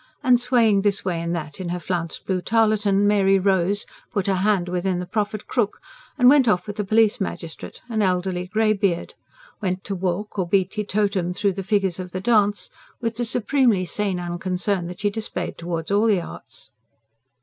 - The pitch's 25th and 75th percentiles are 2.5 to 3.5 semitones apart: Yes, average, 2.9 semitones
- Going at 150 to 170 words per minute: No, average, 185 wpm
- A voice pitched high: Yes, high, 195 Hz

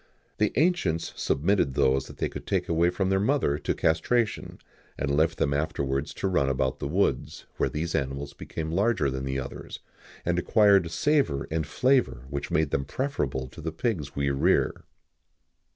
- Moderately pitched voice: No, very low, 80 Hz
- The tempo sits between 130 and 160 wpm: No, average, 170 wpm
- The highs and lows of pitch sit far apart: Yes, wide, 5.9 semitones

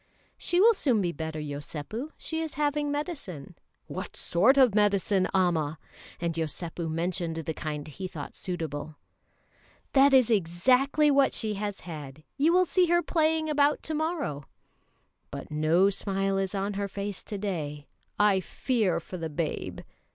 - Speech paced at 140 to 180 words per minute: Yes, average, 155 wpm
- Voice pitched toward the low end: No, high, 195 Hz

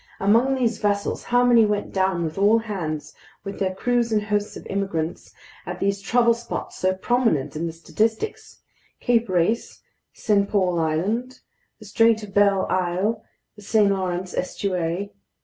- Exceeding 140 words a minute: Yes, average, 155 wpm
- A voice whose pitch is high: Yes, high, 200 Hz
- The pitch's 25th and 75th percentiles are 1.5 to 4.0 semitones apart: Yes, average, 3.7 semitones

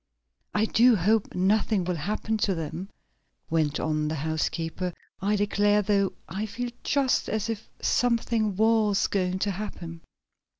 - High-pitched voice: Yes, high, 200 Hz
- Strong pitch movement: No, average, 3.7 semitones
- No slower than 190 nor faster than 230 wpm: No, average, 140 wpm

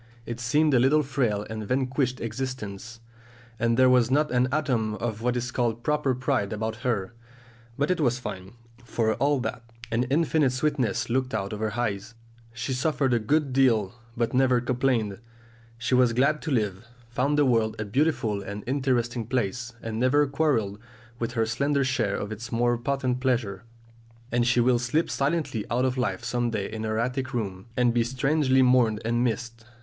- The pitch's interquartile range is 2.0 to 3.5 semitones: Yes, average, 2.8 semitones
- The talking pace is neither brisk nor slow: Yes, average, 180 wpm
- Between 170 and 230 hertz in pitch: No, low, 120 Hz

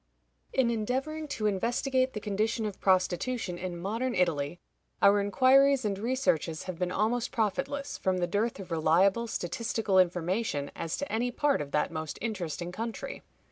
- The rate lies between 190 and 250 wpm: No, average, 155 wpm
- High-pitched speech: Yes, high, 210 Hz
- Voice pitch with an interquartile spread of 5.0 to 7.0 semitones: Yes, average, 5.3 semitones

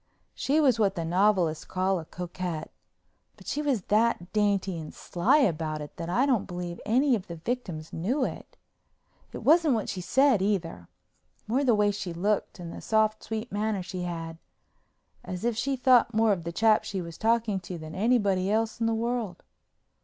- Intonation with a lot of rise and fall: No, average, 4.7 semitones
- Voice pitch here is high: Yes, high, 205 Hz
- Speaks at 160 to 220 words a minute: Yes, average, 190 wpm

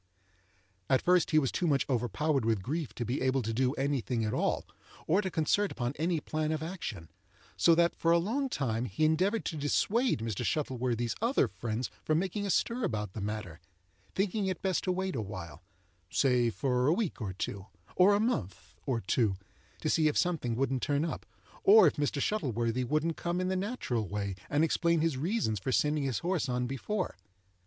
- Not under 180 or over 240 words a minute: Yes, average, 195 wpm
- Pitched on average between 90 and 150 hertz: Yes, medium, 140 Hz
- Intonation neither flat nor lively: No, wide, 7.2 semitones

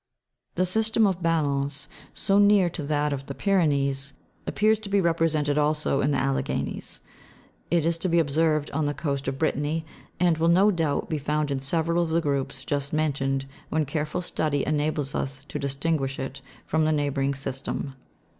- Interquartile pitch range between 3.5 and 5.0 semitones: No, average, 3.1 semitones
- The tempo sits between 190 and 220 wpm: No, average, 175 wpm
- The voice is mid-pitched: Yes, medium, 150 Hz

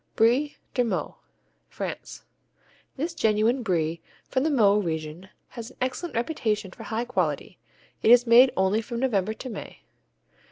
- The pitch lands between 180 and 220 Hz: No, high, 230 Hz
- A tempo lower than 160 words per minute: Yes, average, 150 wpm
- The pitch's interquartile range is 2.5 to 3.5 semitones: No, average, 4.1 semitones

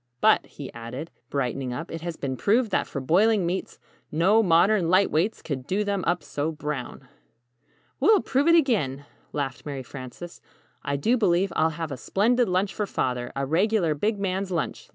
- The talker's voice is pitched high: No, medium, 170 Hz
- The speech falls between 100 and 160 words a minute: No, average, 180 wpm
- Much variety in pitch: Yes, wide, 6.1 semitones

